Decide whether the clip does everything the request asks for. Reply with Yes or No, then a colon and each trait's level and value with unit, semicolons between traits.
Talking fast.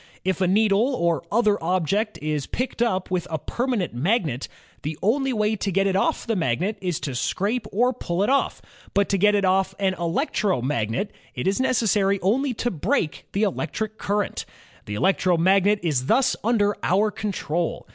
No: average, 175 wpm